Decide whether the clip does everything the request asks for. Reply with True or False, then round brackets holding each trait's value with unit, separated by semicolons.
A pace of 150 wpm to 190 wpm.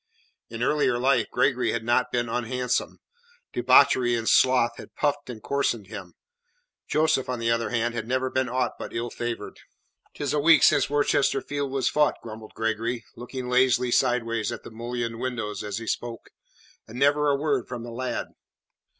True (175 wpm)